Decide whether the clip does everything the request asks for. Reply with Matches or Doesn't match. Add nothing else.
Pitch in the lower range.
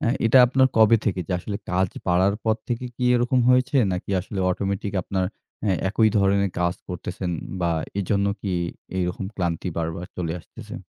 Matches